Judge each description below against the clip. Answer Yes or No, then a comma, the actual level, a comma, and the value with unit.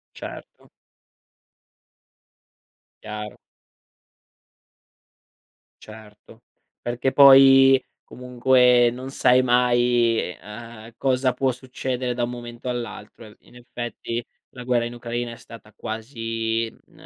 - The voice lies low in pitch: Yes, low, 120 Hz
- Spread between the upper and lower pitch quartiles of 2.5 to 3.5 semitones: No, narrow, 1.7 semitones